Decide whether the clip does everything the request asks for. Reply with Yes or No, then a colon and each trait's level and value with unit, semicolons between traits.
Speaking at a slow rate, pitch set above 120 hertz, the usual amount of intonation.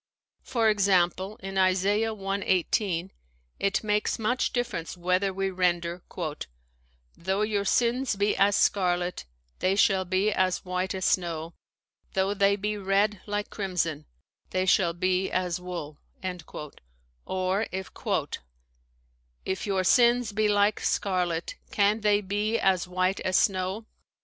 No: slow, 125 wpm; high, 190 Hz; narrow, 2.3 semitones